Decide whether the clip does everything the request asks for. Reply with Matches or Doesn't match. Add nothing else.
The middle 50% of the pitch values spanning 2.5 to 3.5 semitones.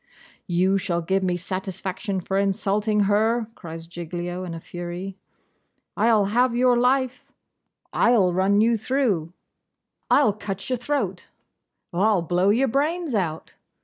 Doesn't match